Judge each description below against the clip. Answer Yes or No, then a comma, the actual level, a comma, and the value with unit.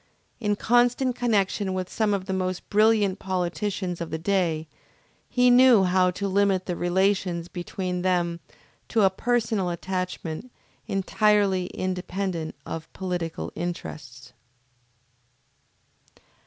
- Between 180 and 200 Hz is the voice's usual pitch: Yes, medium, 185 Hz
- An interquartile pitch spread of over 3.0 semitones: No, average, 2.7 semitones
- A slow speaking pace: Yes, slow, 115 wpm